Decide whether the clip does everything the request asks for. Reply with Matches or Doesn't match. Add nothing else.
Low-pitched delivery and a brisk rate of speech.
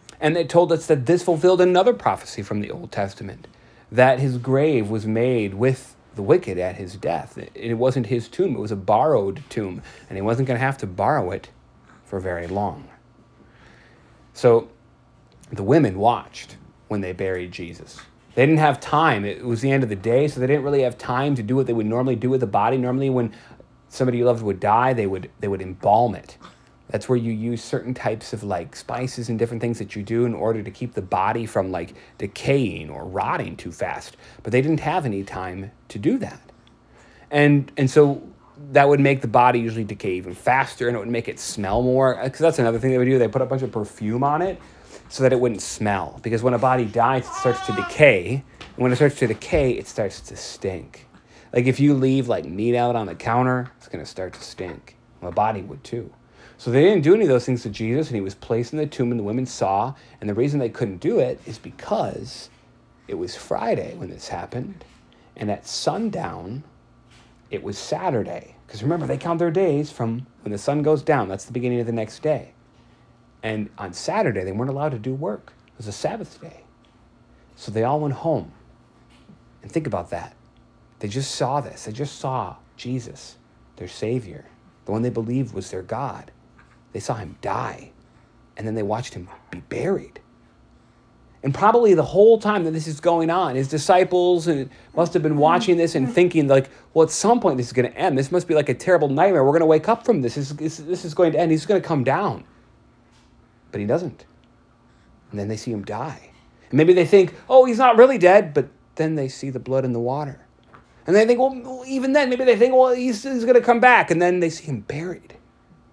Matches